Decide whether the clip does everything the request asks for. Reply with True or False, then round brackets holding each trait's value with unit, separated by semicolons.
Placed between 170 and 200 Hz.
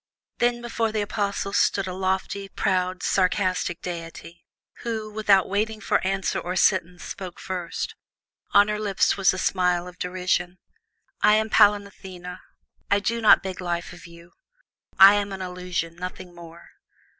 True (185 Hz)